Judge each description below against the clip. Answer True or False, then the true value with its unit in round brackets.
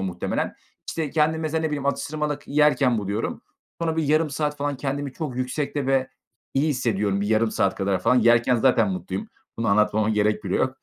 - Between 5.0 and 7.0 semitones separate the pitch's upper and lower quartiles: True (5.4 semitones)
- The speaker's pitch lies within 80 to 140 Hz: True (135 Hz)